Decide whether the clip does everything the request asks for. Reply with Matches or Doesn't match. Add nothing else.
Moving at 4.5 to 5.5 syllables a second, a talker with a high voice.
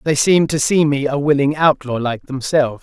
Doesn't match